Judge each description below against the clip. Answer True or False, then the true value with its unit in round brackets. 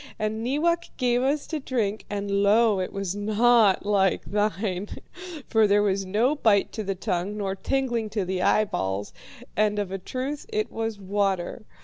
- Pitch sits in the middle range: False (210 Hz)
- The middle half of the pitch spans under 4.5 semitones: True (3.2 semitones)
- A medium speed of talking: True (165 wpm)